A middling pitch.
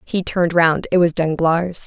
Yes: medium, 170 Hz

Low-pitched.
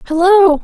No: very high, 355 Hz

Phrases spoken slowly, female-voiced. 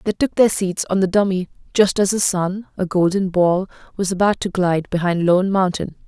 No: fast, 205 wpm; female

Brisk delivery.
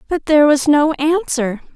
No: average, 170 wpm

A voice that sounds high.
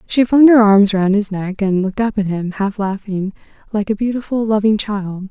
Yes: high, 205 Hz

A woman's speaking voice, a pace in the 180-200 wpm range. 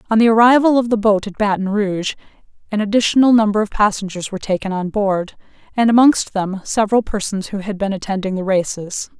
Yes: female; average, 190 wpm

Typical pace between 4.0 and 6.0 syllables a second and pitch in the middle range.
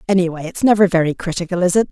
No: 7.4 syllables/s; medium, 180 Hz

